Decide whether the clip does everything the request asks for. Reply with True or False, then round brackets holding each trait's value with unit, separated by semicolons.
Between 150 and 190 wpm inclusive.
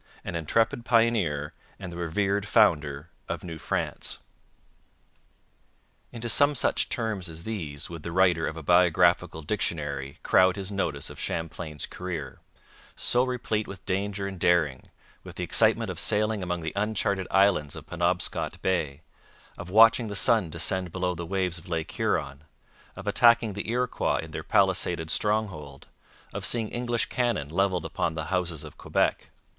True (155 wpm)